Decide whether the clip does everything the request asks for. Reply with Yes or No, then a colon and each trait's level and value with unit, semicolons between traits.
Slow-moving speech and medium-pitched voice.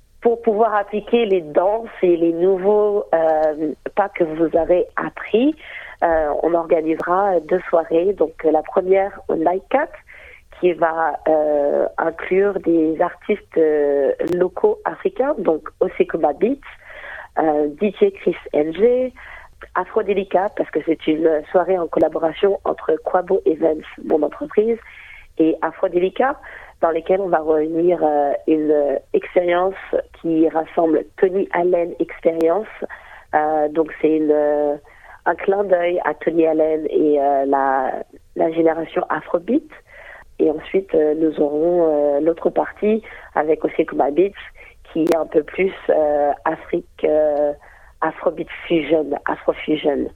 Yes: slow, 130 wpm; medium, 170 Hz